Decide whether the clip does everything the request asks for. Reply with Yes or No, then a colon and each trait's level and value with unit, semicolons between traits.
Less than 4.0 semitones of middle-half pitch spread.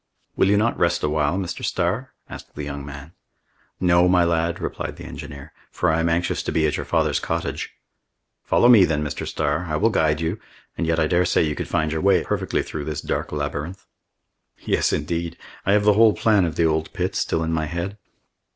Yes: average, 2.8 semitones